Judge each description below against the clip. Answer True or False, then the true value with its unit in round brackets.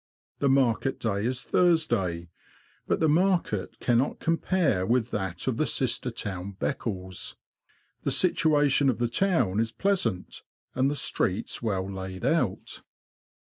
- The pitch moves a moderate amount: False (7.2 semitones)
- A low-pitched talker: True (120 Hz)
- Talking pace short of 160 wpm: True (135 wpm)